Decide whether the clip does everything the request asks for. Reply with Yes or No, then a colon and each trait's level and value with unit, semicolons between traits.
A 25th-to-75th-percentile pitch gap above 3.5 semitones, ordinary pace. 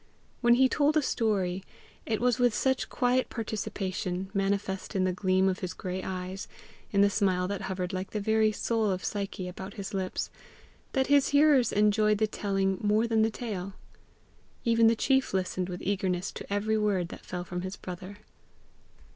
No: average, 3.2 semitones; average, 180 wpm